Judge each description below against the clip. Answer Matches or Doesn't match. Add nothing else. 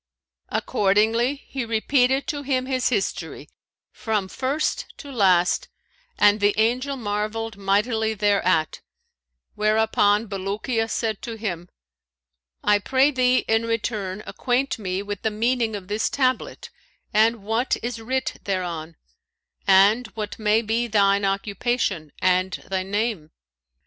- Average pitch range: Matches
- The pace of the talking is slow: Matches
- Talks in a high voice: Matches